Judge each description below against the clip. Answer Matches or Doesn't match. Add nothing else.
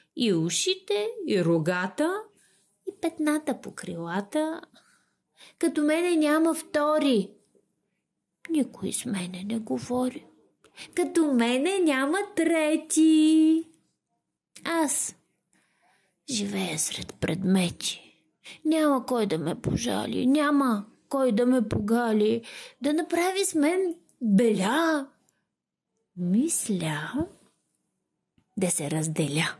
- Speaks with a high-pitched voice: Matches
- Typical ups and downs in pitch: Doesn't match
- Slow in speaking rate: Matches